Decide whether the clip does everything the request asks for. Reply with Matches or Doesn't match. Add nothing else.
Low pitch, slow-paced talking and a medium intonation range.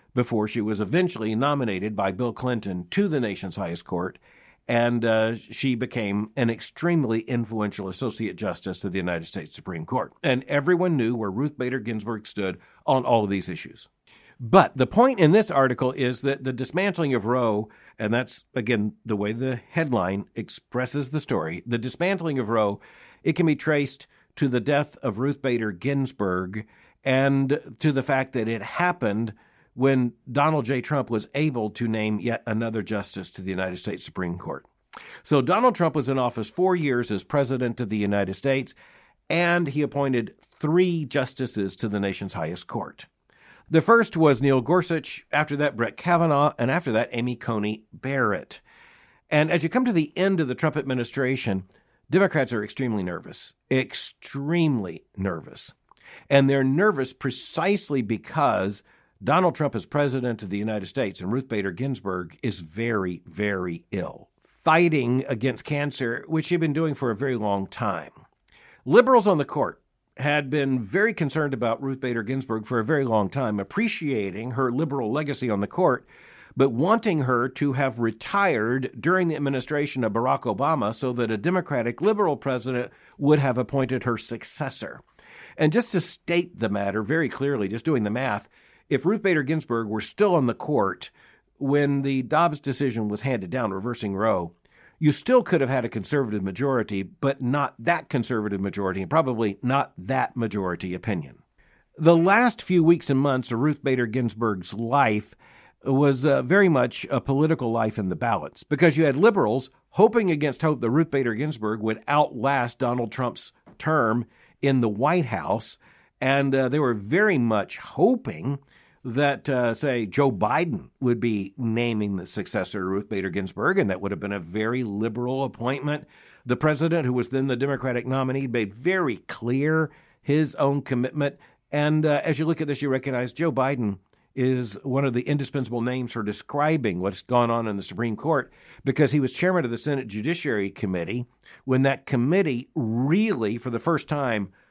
Doesn't match